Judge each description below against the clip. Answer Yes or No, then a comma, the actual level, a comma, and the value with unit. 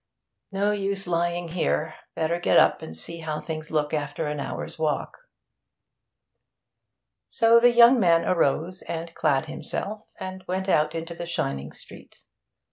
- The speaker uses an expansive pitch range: No, average, 3.4 semitones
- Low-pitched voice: No, medium, 170 Hz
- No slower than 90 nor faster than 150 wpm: Yes, average, 145 wpm